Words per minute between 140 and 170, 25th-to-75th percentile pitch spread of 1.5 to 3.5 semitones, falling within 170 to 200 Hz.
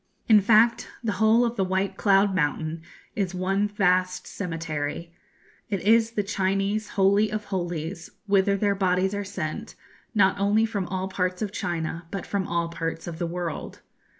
Yes: average, 165 wpm; average, 2.8 semitones; high, 190 Hz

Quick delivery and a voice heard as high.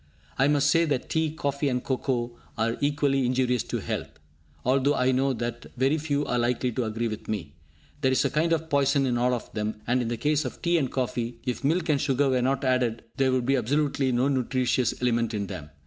No: fast, 225 wpm; low, 130 Hz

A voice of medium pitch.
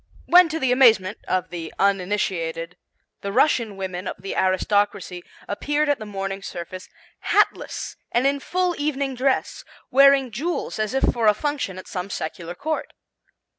No: high, 210 Hz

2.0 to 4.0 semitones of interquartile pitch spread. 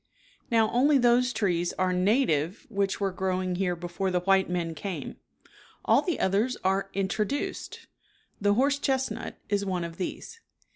No: average, 4.6 semitones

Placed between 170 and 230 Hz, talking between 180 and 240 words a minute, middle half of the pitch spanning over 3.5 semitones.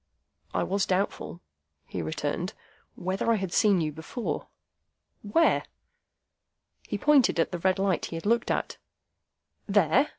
No: high, 190 Hz; slow, 135 wpm; average, 4.2 semitones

